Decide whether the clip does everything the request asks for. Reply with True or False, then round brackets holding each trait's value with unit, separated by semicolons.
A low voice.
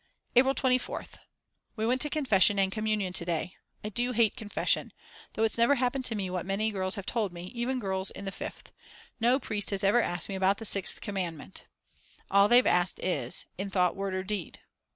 False (200 Hz)